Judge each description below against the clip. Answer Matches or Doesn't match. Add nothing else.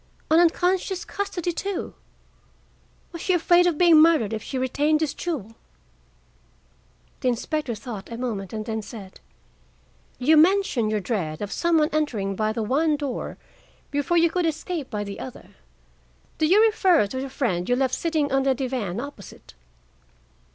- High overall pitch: Matches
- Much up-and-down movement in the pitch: Matches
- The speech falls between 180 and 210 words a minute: Doesn't match